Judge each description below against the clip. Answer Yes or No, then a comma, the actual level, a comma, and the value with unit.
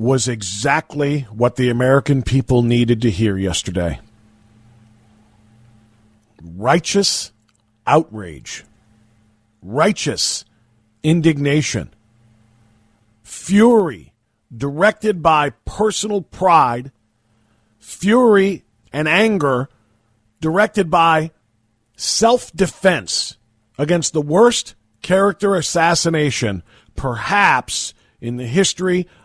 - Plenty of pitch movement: Yes, wide, 7.0 semitones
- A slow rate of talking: Yes, slow, 70 wpm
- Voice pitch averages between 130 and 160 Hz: No, low, 120 Hz